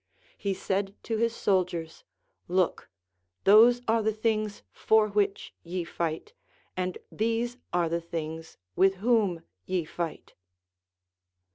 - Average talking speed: No, slow, 120 wpm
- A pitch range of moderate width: Yes, average, 4.1 semitones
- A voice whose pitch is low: No, high, 195 Hz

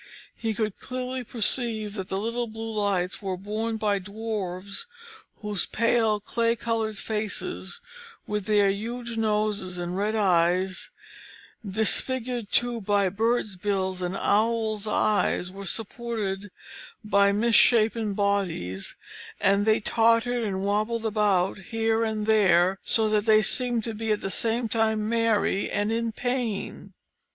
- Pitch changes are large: No, narrow, 2.4 semitones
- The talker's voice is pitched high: Yes, high, 215 Hz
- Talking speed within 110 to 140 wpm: Yes, slow, 135 wpm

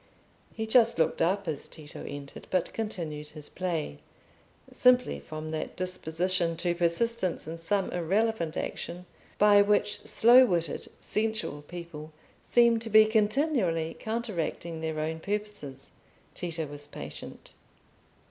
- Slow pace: Yes, slow, 125 wpm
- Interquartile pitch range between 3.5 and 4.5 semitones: No, average, 5.2 semitones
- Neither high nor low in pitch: Yes, medium, 175 Hz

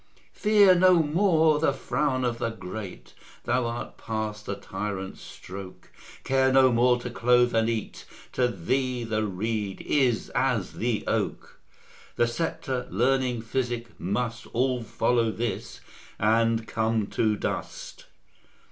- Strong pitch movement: No, average, 3.0 semitones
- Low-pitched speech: Yes, low, 120 Hz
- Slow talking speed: Yes, slow, 130 wpm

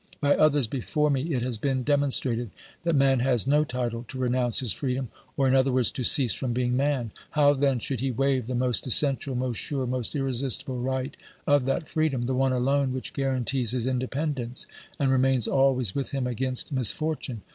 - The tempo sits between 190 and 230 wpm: Yes, average, 200 wpm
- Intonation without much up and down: Yes, narrow, 1.8 semitones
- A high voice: No, low, 130 Hz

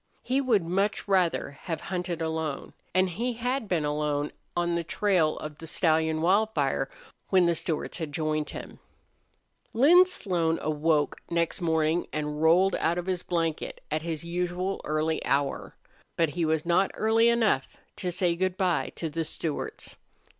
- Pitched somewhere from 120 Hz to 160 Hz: No, medium, 170 Hz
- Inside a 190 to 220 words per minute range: No, average, 160 wpm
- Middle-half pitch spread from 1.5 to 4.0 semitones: Yes, average, 3.1 semitones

